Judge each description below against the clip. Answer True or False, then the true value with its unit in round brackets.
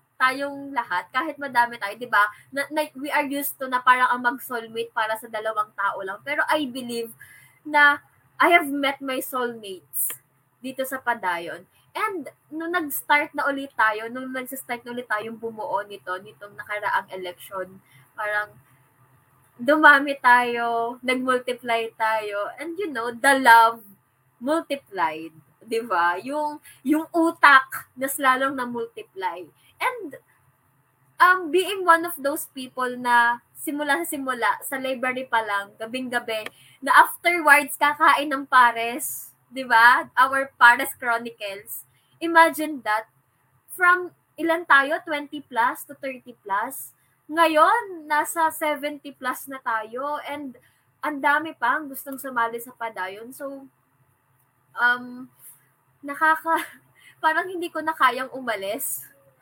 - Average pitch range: True (4.5 semitones)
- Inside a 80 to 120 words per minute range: False (130 wpm)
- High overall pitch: True (260 Hz)